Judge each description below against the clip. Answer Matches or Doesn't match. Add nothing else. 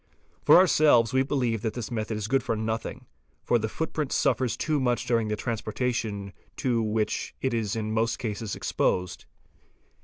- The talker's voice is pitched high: Doesn't match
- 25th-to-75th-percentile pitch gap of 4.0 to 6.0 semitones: Doesn't match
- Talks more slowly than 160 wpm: Doesn't match